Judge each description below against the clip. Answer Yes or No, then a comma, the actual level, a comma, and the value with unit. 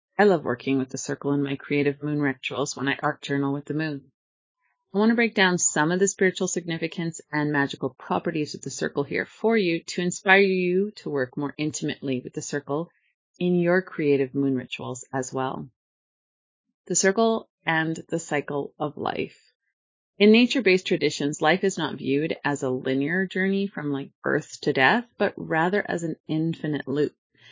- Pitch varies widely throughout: No, average, 4.7 semitones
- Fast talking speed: No, average, 180 wpm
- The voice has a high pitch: No, medium, 150 Hz